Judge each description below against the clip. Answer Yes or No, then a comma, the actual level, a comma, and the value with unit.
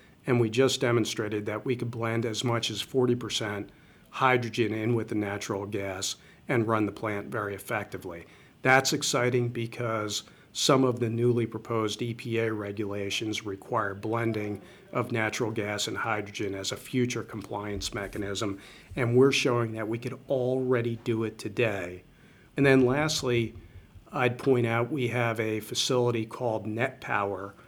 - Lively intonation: No, average, 2.9 semitones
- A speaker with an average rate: Yes, average, 145 wpm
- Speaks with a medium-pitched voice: No, low, 115 Hz